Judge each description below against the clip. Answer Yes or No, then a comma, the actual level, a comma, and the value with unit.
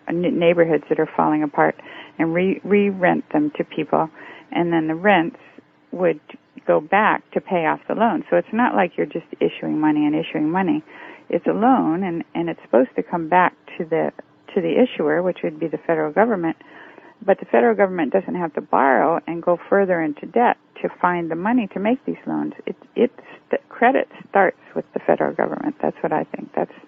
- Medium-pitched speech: Yes, medium, 170 Hz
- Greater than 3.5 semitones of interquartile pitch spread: Yes, average, 3.9 semitones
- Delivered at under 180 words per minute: No, average, 200 wpm